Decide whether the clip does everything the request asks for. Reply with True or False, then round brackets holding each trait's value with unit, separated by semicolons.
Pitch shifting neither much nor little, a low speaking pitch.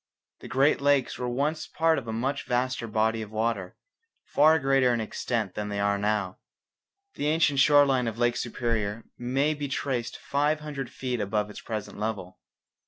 True (4.5 semitones; 120 Hz)